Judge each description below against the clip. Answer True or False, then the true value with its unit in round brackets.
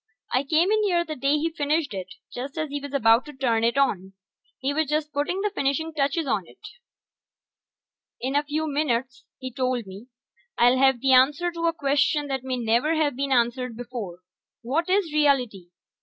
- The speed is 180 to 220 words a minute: True (190 wpm)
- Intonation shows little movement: False (4.0 semitones)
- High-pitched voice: True (275 Hz)